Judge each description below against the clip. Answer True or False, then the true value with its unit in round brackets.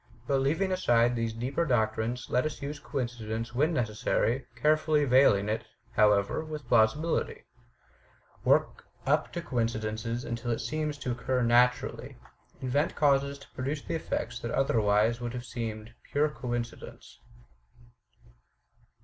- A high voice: False (125 Hz)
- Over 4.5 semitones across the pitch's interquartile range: False (3.7 semitones)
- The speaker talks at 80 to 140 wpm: True (135 wpm)